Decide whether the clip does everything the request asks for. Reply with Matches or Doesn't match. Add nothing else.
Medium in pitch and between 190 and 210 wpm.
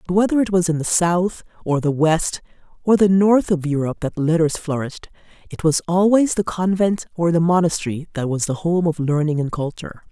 Matches